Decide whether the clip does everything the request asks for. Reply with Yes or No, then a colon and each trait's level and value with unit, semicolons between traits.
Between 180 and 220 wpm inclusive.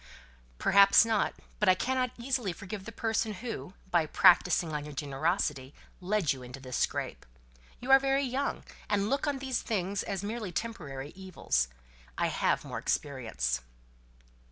No: average, 155 wpm